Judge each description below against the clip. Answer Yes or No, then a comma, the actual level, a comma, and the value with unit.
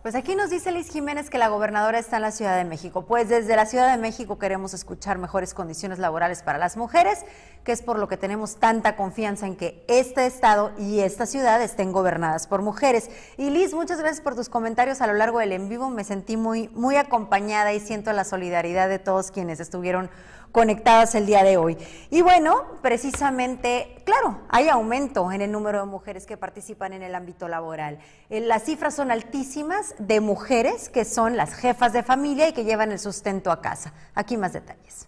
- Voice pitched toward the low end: No, high, 220 Hz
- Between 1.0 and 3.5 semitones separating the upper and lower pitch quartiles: No, average, 4.3 semitones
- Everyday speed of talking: No, fast, 200 wpm